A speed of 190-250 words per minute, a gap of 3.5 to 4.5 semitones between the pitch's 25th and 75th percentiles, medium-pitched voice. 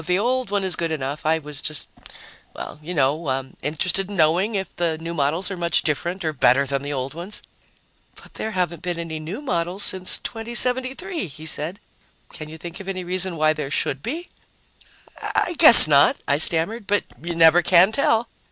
Yes: average, 195 wpm; average, 4.1 semitones; medium, 170 Hz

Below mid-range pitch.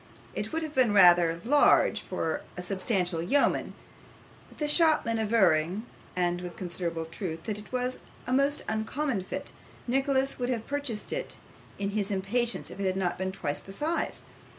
No: high, 210 Hz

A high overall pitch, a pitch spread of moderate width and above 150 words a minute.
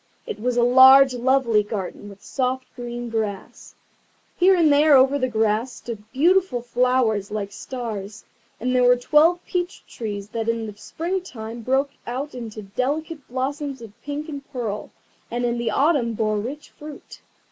Yes: high, 245 Hz; average, 4.1 semitones; average, 165 wpm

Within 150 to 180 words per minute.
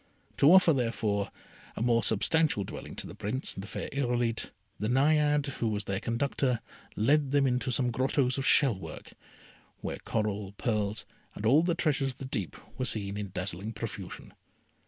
Yes: average, 175 wpm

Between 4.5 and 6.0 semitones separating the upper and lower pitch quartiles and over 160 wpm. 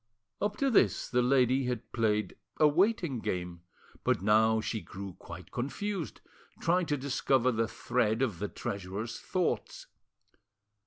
No: wide, 5.4 semitones; average, 140 wpm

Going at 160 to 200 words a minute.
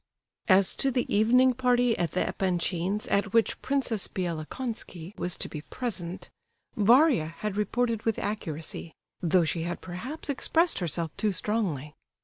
No: average, 140 wpm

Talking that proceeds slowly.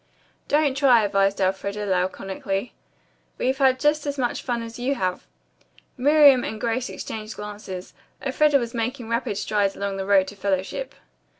No: average, 155 wpm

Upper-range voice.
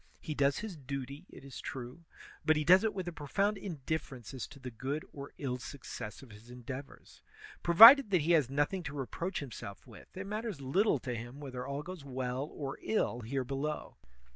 No: medium, 140 Hz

